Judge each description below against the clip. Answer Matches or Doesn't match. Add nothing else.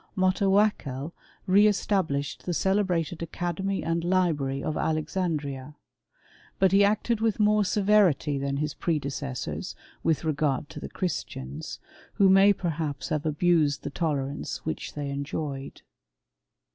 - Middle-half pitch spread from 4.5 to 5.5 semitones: Matches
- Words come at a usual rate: Doesn't match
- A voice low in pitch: Doesn't match